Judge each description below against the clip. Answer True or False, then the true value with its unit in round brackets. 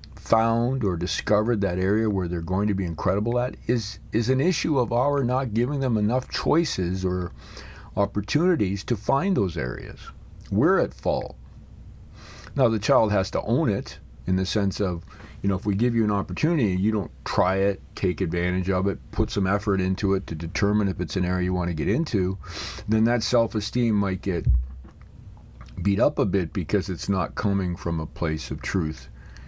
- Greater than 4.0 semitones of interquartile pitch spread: False (3.3 semitones)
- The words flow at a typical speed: True (190 wpm)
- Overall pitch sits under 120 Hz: True (100 Hz)